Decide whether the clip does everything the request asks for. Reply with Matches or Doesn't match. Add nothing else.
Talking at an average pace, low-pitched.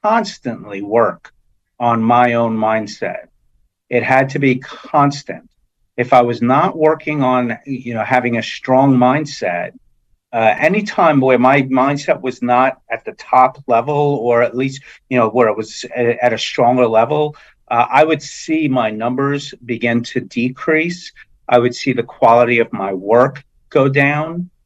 Matches